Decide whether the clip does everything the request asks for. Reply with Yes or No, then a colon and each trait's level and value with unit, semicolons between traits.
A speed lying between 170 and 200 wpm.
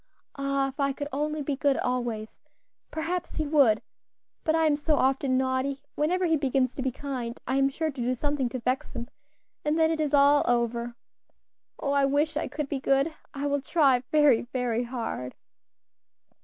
Yes: average, 185 wpm